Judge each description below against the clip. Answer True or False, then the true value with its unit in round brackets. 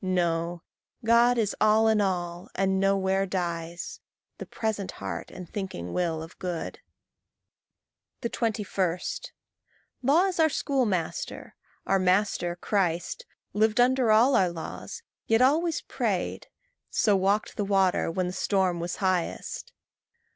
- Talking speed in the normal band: False (125 wpm)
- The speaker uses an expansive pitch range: False (4.0 semitones)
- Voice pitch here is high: True (195 Hz)